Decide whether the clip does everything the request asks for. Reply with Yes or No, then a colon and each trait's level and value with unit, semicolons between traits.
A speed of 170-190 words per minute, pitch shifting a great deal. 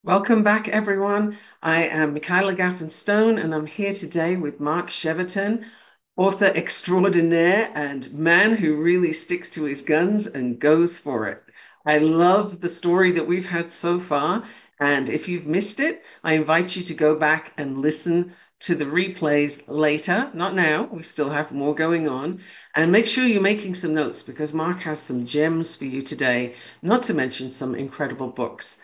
No: average, 175 wpm; average, 3.4 semitones